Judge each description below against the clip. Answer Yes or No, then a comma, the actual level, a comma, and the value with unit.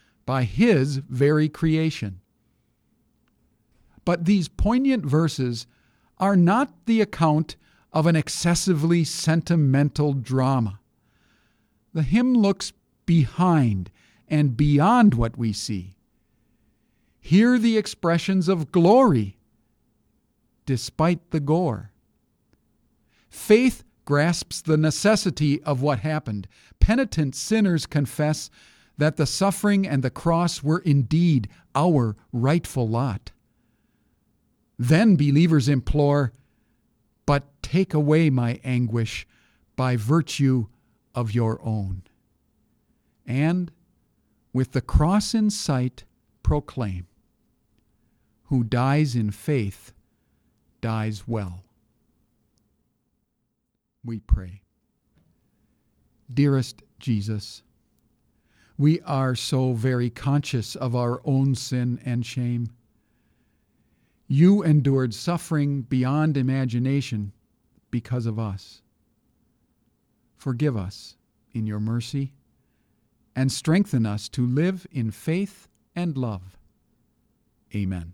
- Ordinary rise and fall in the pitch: No, wide, 5.8 semitones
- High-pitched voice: No, low, 135 Hz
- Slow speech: Yes, slow, 90 wpm